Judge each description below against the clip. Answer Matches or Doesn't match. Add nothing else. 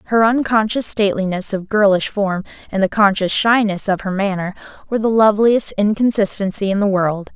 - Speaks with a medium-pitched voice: Doesn't match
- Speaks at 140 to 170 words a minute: Matches